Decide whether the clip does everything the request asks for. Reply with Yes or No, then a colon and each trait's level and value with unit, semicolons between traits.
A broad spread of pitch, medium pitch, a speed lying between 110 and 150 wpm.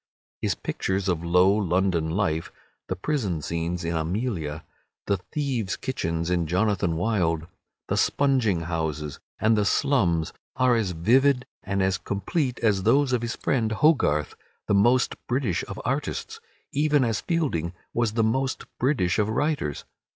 No: wide, 6.9 semitones; low, 100 Hz; average, 145 wpm